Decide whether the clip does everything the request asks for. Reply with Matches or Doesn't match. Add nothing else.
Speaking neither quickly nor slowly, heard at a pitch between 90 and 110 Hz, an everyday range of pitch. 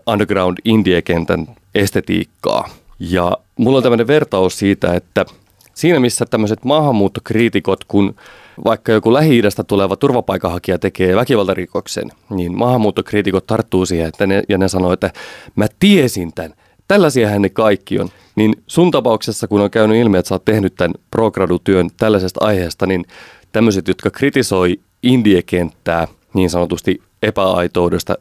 Matches